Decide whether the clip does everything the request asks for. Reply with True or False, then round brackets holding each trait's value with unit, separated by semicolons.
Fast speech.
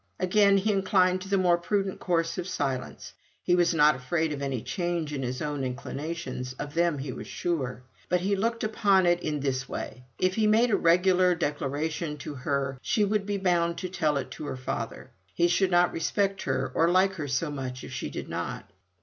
True (210 wpm)